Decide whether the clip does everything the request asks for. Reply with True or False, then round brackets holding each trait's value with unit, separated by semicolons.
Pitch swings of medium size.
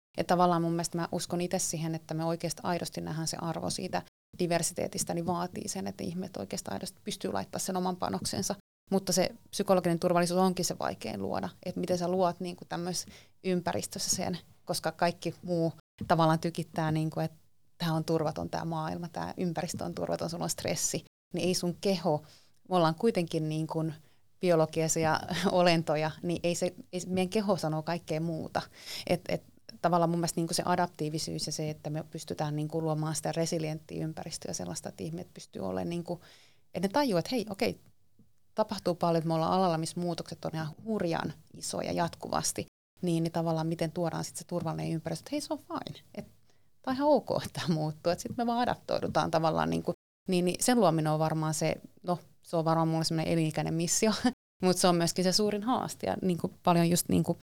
False (2.2 semitones)